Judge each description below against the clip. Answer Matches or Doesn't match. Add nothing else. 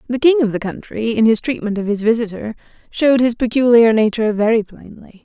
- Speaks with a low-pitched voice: Doesn't match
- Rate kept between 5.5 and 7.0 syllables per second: Matches